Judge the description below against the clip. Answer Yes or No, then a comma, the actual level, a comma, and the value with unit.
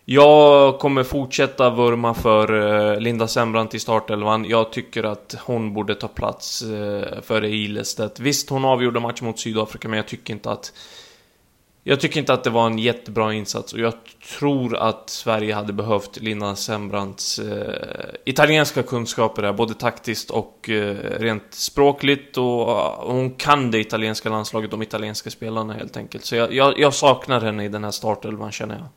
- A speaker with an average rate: Yes, average, 160 wpm